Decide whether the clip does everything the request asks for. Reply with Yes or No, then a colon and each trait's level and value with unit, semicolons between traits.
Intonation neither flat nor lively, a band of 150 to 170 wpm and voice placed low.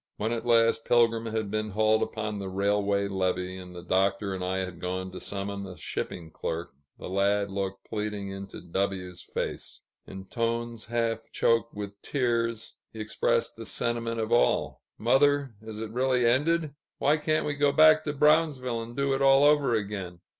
No: average, 3.5 semitones; average, 180 wpm; low, 110 Hz